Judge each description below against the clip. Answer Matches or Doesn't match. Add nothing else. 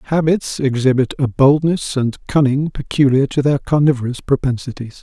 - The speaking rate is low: Matches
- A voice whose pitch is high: Doesn't match